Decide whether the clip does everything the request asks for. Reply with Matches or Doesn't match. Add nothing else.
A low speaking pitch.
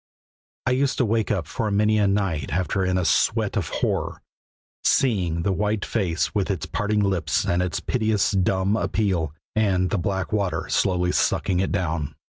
Matches